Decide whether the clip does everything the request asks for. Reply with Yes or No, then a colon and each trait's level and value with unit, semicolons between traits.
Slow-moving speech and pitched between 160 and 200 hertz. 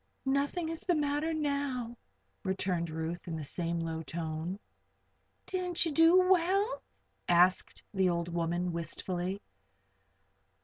Yes: slow, 120 wpm; high, 190 Hz